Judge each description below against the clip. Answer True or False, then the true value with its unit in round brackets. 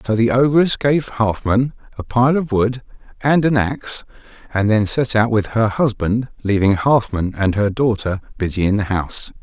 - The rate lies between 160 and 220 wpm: True (180 wpm)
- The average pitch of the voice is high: False (115 Hz)